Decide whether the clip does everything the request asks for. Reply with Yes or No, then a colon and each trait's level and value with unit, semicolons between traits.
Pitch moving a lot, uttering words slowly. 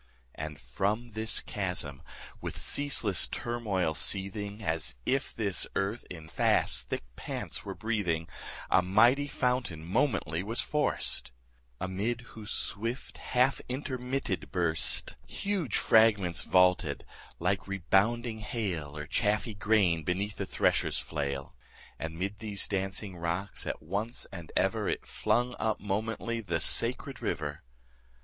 No: average, 5.0 semitones; slow, 125 wpm